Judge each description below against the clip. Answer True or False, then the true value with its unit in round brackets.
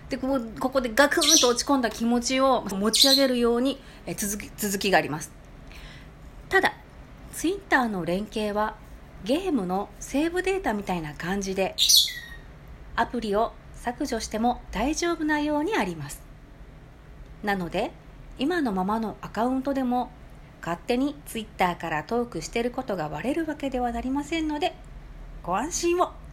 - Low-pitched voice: False (240 Hz)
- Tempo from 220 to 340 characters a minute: True (310 characters per minute)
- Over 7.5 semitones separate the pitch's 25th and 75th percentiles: False (5.4 semitones)